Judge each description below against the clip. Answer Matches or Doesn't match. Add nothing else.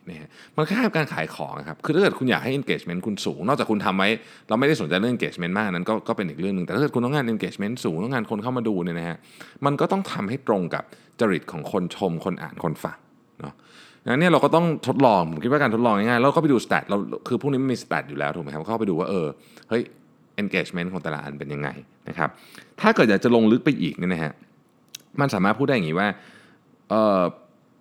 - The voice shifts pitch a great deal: Matches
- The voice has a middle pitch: Doesn't match